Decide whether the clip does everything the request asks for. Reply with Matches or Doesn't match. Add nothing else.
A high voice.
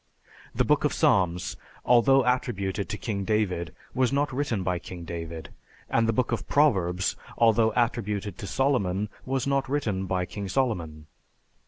Doesn't match